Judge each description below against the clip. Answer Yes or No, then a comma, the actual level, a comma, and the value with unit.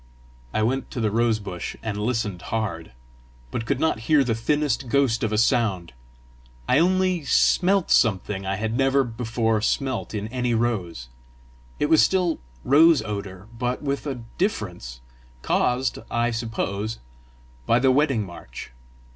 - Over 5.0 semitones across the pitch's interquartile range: No, average, 4.4 semitones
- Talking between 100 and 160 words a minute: Yes, average, 145 wpm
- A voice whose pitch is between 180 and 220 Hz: No, low, 115 Hz